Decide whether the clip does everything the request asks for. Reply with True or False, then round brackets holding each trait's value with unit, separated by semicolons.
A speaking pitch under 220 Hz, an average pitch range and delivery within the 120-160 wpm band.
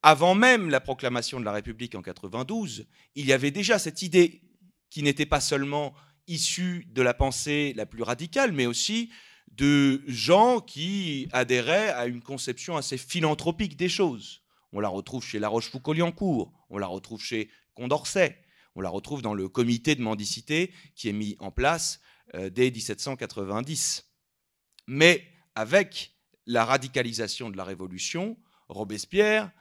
False (135 Hz; 6.7 semitones; 150 wpm)